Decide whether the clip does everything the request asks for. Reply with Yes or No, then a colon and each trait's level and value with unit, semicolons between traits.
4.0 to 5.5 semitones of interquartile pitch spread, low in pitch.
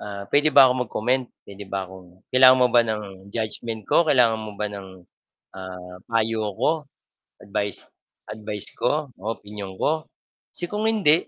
Yes: average, 4.3 semitones; low, 110 Hz